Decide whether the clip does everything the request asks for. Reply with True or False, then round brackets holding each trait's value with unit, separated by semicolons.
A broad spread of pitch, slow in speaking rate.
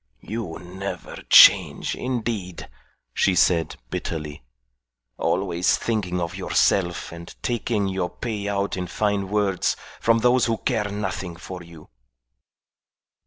False (3.4 semitones; 120 wpm)